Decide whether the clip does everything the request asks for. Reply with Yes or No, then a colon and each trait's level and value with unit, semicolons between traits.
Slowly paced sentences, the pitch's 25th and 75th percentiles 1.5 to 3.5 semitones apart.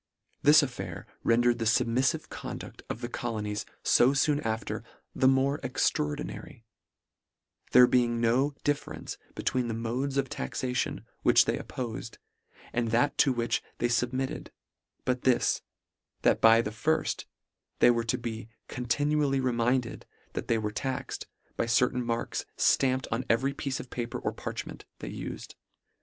No: average, 150 wpm; narrow, 2.4 semitones